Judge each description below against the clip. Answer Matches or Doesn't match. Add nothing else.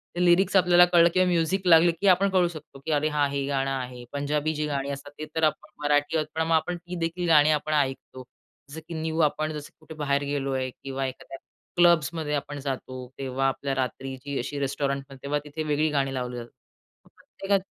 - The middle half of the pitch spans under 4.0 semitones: Matches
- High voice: Doesn't match